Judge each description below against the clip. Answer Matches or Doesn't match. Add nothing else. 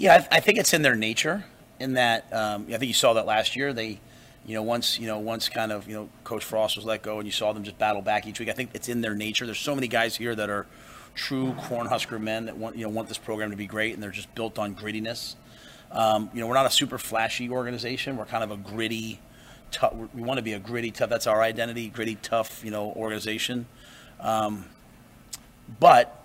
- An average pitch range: Doesn't match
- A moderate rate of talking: Doesn't match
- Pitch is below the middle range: Matches